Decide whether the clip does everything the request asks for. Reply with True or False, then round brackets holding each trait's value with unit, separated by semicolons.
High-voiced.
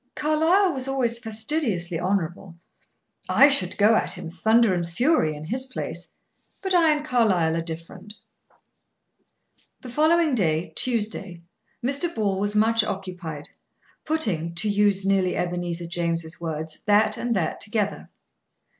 True (205 Hz)